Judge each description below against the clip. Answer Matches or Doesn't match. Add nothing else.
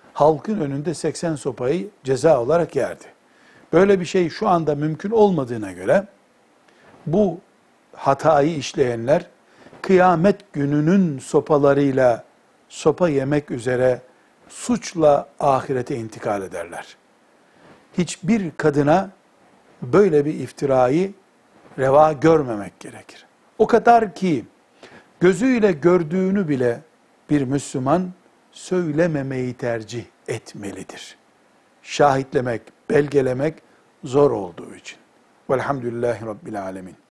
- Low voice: Doesn't match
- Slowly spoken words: Matches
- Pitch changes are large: Doesn't match